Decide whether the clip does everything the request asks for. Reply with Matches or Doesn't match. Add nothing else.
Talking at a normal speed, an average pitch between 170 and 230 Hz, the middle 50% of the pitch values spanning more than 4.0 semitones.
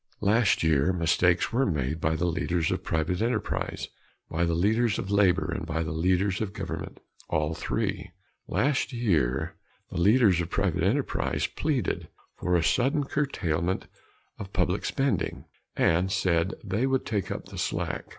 Doesn't match